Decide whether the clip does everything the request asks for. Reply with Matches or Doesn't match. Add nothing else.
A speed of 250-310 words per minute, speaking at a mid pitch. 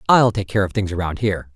Doesn't match